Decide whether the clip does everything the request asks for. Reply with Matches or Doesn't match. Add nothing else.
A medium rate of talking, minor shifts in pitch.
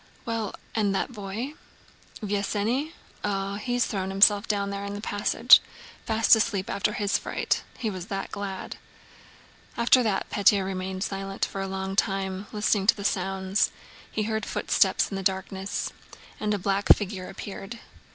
Matches